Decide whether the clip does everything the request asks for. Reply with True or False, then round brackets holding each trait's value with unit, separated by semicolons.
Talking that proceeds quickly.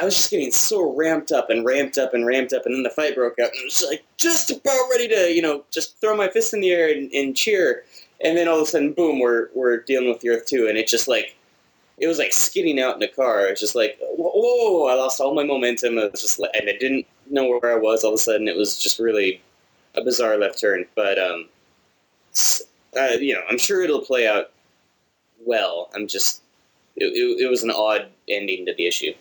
True (255 wpm)